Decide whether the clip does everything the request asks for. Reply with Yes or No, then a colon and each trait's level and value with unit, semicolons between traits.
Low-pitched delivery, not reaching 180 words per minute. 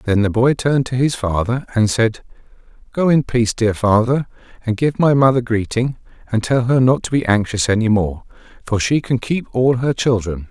No: low, 120 Hz; average, 200 wpm